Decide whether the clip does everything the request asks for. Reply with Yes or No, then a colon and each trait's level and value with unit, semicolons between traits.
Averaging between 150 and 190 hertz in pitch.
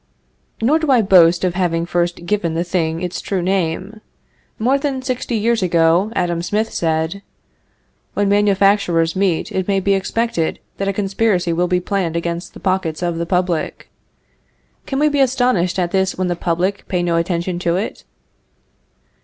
Yes: medium, 185 Hz